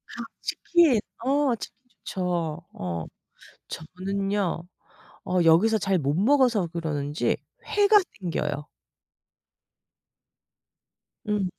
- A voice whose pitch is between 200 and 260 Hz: No, medium, 185 Hz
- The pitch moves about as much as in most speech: No, wide, 5.7 semitones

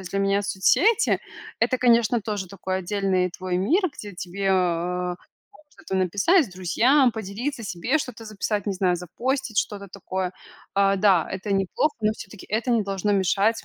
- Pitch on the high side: Yes, high, 200 Hz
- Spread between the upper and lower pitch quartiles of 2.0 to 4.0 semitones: Yes, average, 3.3 semitones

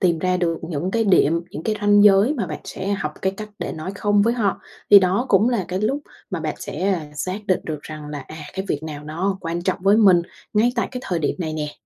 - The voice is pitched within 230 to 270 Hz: No, medium, 185 Hz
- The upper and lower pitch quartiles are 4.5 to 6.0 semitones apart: No, average, 4.0 semitones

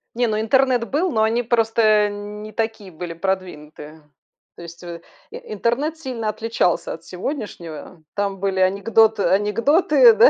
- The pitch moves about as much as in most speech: Yes, average, 3.9 semitones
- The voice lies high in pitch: Yes, high, 215 Hz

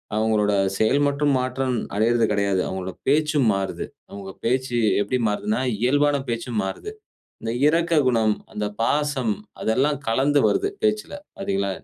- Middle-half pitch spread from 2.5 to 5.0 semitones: No, wide, 5.6 semitones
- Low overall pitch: Yes, low, 125 Hz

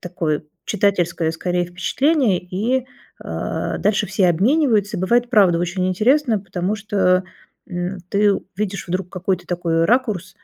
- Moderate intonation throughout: Yes, average, 3.2 semitones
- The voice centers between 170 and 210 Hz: Yes, high, 190 Hz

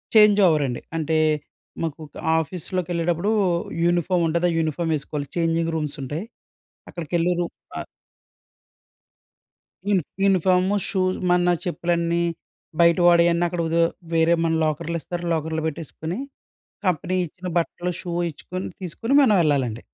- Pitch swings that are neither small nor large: No, narrow, 1.9 semitones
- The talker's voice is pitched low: No, medium, 170 Hz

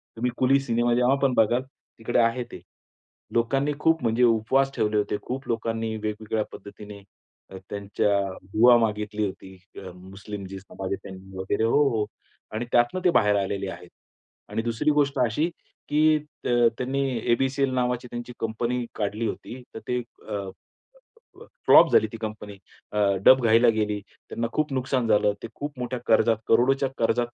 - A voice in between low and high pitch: No, low, 115 Hz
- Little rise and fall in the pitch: No, average, 3.2 semitones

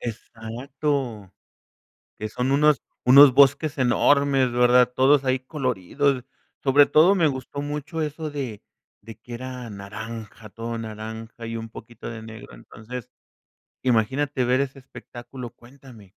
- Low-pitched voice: Yes, low, 125 Hz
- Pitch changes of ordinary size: Yes, average, 3.7 semitones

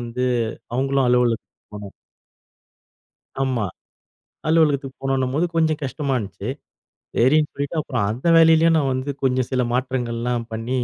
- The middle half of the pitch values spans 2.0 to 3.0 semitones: Yes, average, 2.7 semitones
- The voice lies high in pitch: No, low, 130 Hz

